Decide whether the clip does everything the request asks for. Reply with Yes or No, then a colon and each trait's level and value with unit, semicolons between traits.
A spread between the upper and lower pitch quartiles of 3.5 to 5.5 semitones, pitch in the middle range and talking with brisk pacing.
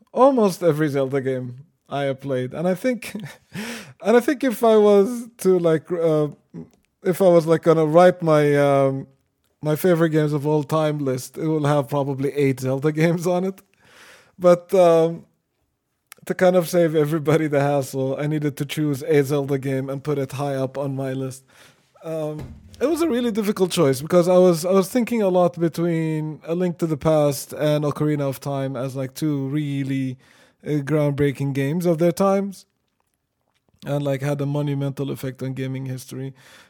No: average, 4.0 semitones; medium, 150 Hz; average, 180 wpm